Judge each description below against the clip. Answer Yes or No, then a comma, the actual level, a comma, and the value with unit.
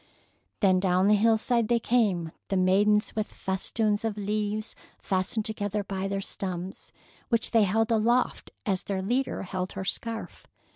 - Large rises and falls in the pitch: No, average, 2.7 semitones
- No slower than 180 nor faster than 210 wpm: No, average, 150 wpm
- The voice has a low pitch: No, high, 205 Hz